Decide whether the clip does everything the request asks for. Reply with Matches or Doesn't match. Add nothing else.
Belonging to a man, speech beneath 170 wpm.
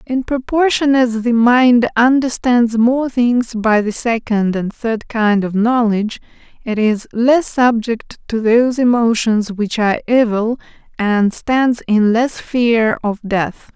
Doesn't match